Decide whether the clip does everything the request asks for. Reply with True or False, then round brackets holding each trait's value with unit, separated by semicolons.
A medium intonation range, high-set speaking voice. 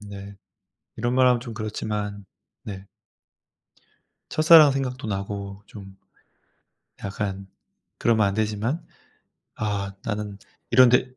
False (3.4 semitones; 105 Hz)